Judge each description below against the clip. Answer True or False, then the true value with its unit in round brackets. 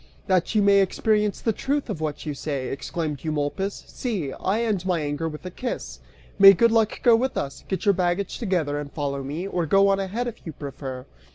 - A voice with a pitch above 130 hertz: True (185 Hz)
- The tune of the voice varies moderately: False (5.9 semitones)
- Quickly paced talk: True (210 wpm)